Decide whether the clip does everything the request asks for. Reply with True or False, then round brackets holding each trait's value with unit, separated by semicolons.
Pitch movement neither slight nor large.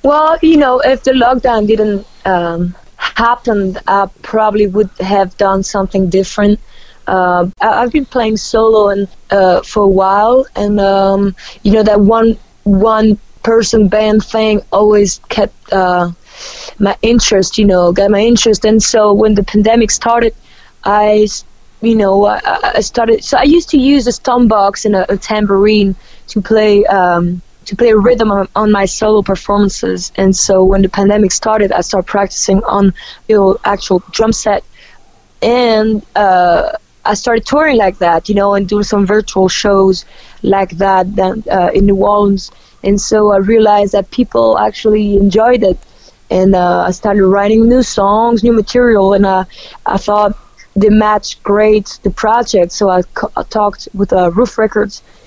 False (2.3 semitones)